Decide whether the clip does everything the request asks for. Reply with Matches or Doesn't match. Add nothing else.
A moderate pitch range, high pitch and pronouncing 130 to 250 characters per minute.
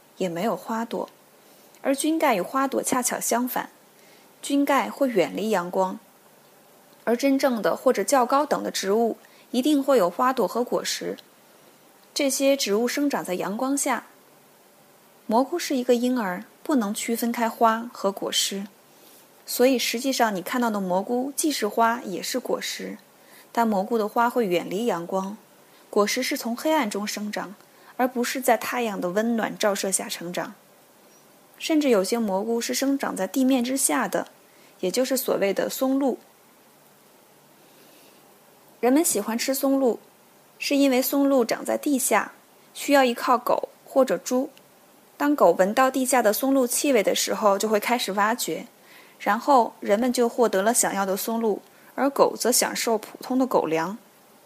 Matches